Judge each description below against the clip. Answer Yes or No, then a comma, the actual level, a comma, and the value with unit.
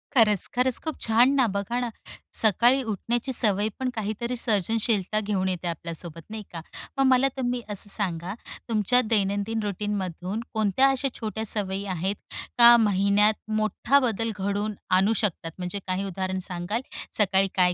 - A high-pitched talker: Yes, high, 210 Hz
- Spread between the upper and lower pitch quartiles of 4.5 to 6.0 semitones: No, average, 3.3 semitones